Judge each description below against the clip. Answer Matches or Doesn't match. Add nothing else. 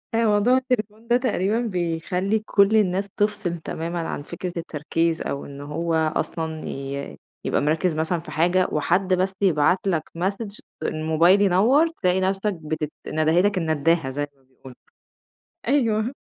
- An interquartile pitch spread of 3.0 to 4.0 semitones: Doesn't match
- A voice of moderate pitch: Matches